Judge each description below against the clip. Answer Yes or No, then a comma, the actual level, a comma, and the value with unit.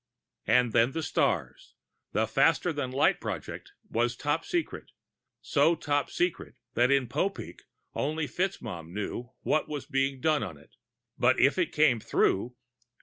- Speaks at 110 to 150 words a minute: Yes, average, 145 wpm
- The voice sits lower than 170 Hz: Yes, low, 135 Hz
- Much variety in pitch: No, average, 4.3 semitones